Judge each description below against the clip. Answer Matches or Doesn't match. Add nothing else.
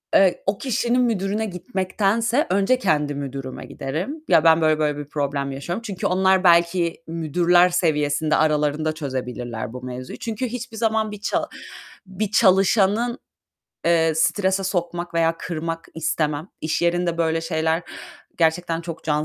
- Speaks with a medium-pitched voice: Matches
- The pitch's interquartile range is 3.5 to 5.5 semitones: Matches